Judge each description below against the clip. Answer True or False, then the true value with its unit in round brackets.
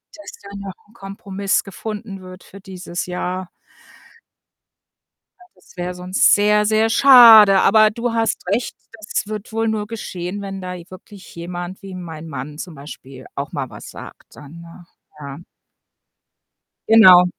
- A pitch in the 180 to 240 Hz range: True (190 Hz)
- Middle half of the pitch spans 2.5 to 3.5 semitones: True (3.2 semitones)